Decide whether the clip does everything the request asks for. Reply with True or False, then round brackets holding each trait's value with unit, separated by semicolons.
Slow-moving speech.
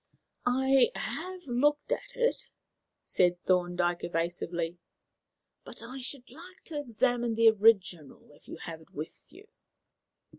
True (125 wpm)